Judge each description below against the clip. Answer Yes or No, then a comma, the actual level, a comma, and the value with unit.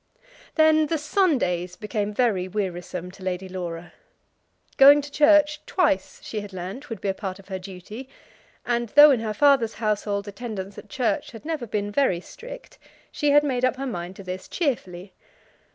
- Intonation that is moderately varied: No, wide, 7.1 semitones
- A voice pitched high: Yes, high, 215 Hz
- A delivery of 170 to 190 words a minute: Yes, average, 175 wpm